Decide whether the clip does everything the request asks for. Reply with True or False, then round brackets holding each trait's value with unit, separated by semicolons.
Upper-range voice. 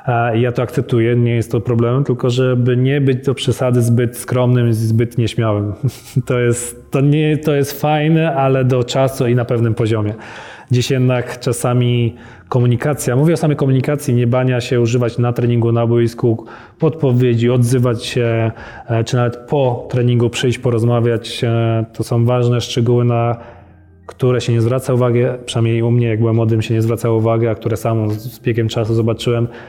False (120 Hz)